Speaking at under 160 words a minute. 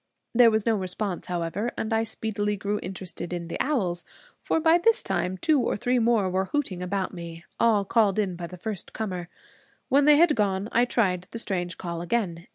No: average, 200 wpm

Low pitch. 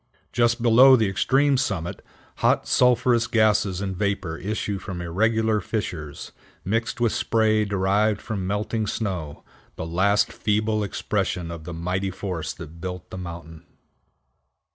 Yes: low, 100 Hz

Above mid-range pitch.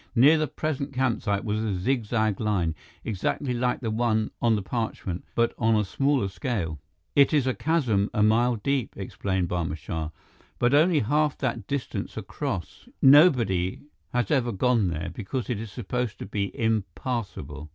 No: low, 115 Hz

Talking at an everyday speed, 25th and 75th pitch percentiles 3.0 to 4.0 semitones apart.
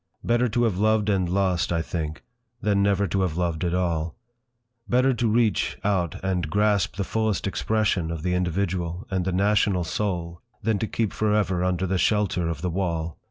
Yes: average, 190 wpm; average, 3.3 semitones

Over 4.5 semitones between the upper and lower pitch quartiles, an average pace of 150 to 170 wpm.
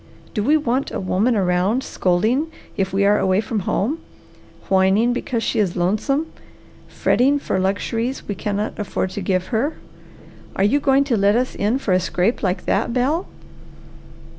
Yes: average, 5.1 semitones; average, 165 wpm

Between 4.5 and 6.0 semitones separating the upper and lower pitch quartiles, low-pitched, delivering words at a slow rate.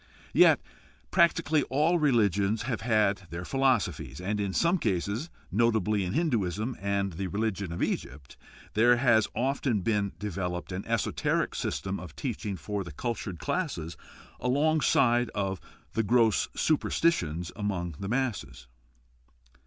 Yes: average, 4.8 semitones; low, 105 Hz; slow, 130 wpm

